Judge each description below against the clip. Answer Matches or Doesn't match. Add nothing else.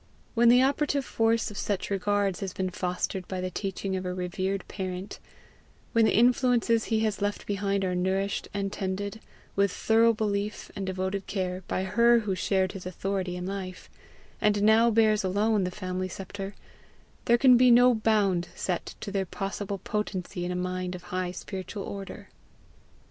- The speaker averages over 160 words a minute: Matches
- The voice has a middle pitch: Doesn't match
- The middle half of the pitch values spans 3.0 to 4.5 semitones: Doesn't match